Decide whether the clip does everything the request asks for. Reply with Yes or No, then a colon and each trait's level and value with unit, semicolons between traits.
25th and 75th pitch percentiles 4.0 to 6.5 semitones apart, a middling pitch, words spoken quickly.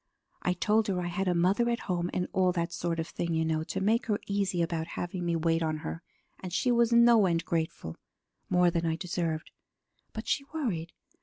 No: average, 3.2 semitones; medium, 175 Hz; fast, 215 wpm